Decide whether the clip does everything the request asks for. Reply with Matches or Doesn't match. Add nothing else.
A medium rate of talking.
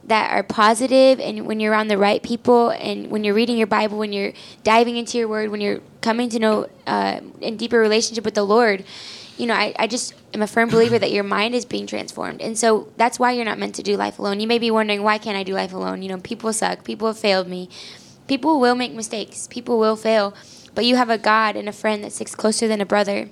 Doesn't match